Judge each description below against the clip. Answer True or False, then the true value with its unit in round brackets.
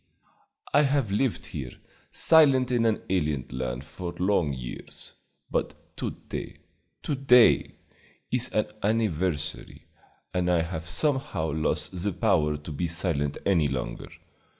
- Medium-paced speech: False (130 wpm)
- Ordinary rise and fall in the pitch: False (7.0 semitones)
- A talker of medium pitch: False (90 Hz)